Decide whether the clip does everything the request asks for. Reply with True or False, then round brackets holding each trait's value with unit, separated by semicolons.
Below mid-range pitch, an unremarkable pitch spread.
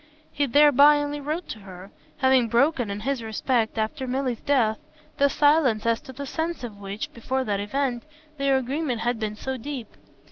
False (260 Hz; 4.2 semitones)